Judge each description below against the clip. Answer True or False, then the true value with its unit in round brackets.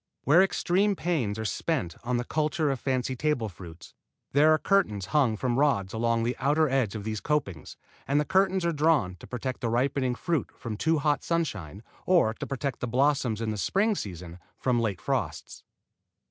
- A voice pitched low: True (130 Hz)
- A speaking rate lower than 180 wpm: False (185 wpm)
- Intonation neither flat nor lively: False (5.8 semitones)